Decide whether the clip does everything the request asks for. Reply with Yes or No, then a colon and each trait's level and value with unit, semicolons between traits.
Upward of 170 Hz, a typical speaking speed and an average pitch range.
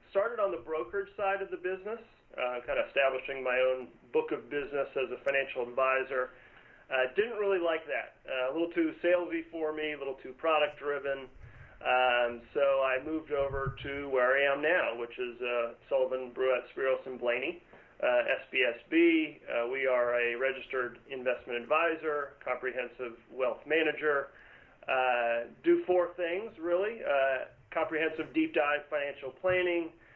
No: medium, 140 Hz; average, 160 wpm; average, 4.7 semitones